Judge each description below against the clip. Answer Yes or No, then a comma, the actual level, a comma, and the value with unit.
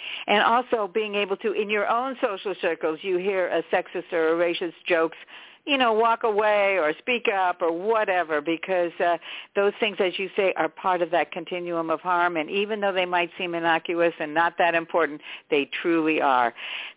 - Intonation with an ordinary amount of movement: Yes, average, 3.5 semitones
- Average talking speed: Yes, average, 195 wpm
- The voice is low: No, medium, 180 Hz